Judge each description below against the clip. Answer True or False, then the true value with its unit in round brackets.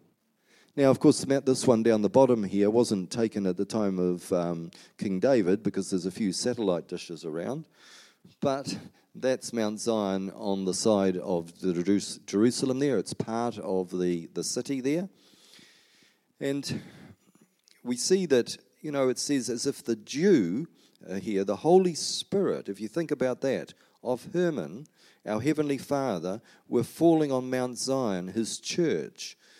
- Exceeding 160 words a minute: False (155 wpm)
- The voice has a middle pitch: False (120 Hz)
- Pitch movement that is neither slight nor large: False (5.9 semitones)